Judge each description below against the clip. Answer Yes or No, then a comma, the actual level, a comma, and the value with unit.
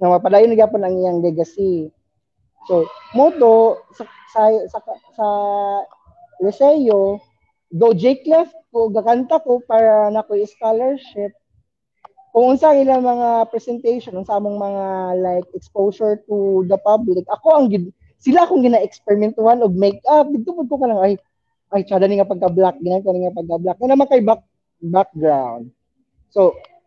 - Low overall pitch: No, high, 215 Hz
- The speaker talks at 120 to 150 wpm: Yes, average, 140 wpm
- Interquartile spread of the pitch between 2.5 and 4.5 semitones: No, average, 4.9 semitones